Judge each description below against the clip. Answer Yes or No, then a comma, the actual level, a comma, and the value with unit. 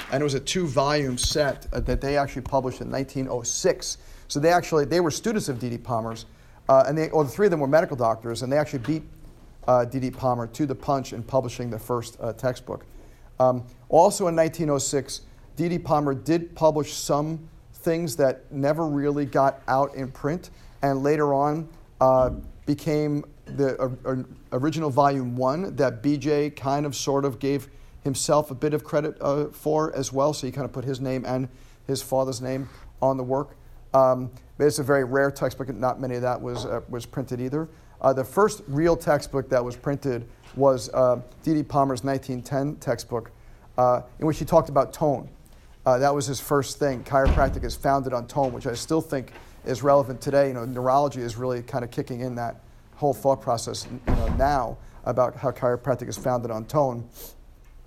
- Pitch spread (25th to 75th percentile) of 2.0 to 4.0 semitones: Yes, average, 2.7 semitones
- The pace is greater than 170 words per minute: Yes, average, 190 wpm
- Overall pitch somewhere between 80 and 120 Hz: No, low, 135 Hz